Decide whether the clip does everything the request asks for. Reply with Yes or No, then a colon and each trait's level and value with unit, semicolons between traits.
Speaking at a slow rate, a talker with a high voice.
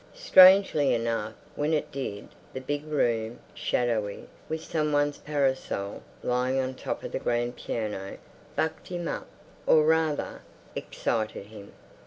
No: slow, 130 wpm; low, 130 Hz